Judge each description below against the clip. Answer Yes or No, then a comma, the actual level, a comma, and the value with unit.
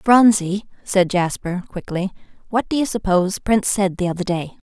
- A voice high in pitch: Yes, high, 195 Hz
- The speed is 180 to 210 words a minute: No, average, 165 wpm